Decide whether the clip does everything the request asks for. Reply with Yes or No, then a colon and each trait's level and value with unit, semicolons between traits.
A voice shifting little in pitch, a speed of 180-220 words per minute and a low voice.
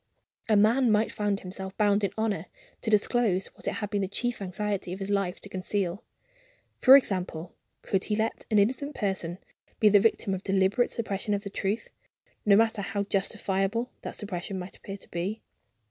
No: narrow, 2.1 semitones; average, 185 wpm; high, 200 Hz